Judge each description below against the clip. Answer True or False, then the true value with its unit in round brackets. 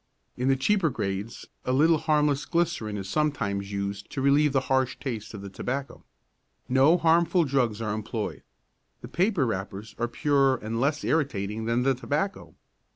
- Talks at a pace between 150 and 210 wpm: True (160 wpm)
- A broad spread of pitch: True (5.7 semitones)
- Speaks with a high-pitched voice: False (130 Hz)